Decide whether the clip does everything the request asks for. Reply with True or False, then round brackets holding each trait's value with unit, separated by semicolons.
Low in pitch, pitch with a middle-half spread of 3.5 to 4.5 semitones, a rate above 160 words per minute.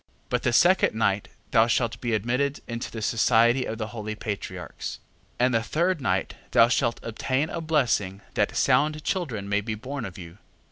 True (115 Hz; 4.1 semitones; 190 wpm)